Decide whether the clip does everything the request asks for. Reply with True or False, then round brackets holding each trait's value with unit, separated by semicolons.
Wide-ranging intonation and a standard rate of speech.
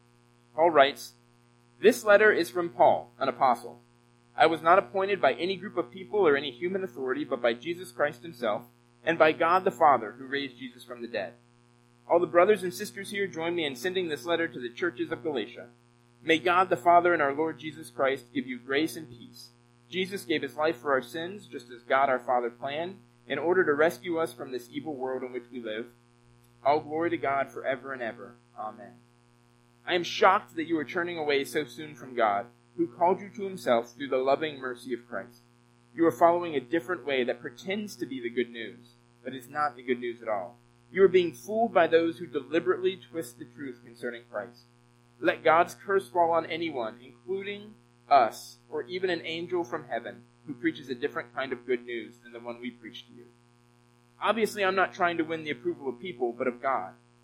False (6.4 semitones; 210 wpm)